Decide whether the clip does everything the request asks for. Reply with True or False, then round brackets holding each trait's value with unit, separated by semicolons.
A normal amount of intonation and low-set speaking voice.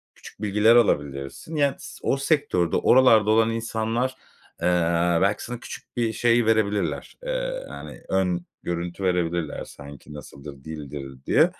False (6.3 semitones; 105 Hz)